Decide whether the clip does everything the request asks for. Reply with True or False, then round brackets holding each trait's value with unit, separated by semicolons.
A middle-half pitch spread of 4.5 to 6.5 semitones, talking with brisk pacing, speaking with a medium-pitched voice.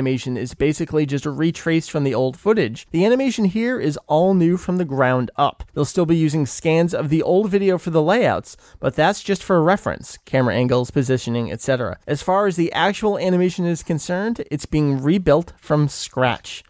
False (5.2 semitones; 195 wpm; 155 Hz)